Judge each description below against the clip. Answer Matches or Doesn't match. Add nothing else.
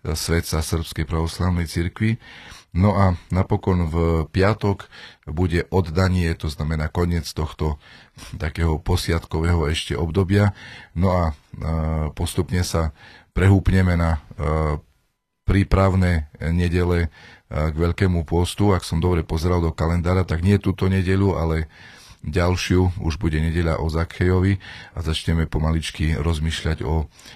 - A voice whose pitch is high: Doesn't match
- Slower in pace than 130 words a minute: Matches